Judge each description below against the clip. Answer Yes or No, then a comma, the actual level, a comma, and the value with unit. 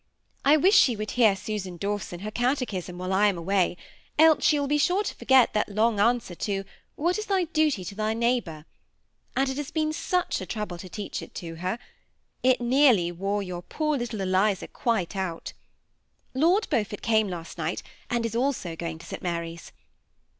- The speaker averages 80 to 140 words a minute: No, average, 200 wpm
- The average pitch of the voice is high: Yes, high, 215 Hz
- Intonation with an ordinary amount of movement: No, wide, 6.3 semitones